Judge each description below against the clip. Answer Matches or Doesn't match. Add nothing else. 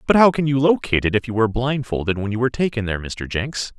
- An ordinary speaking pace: Doesn't match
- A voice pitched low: Matches